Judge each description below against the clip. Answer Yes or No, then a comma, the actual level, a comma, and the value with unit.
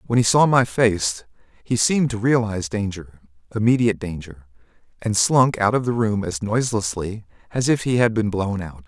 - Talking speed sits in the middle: Yes, average, 170 wpm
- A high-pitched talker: No, low, 105 Hz